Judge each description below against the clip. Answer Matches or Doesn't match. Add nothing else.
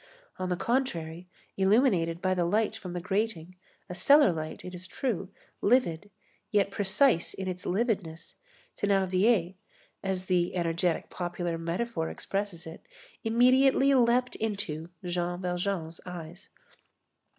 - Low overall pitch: Doesn't match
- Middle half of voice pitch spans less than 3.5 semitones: Doesn't match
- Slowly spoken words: Matches